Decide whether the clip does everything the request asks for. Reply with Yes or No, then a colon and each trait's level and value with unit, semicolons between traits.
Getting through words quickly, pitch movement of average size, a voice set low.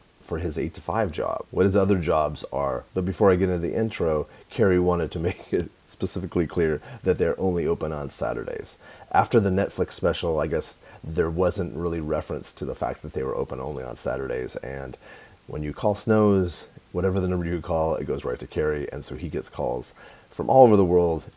Yes: fast, 215 wpm; average, 3.5 semitones; very low, 90 Hz